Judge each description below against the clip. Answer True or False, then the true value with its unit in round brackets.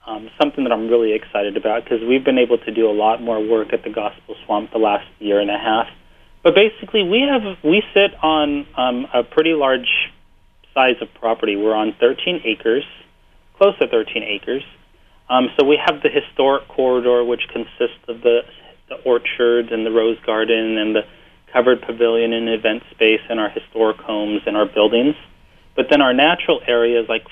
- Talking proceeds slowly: False (190 wpm)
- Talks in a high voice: False (120 Hz)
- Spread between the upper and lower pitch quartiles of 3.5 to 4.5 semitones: False (5.1 semitones)